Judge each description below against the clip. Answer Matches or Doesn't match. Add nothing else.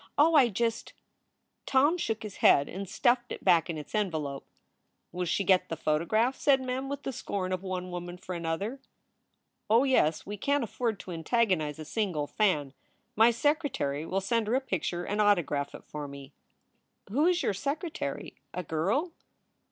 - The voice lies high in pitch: Matches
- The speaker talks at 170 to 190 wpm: Matches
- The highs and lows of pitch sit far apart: Matches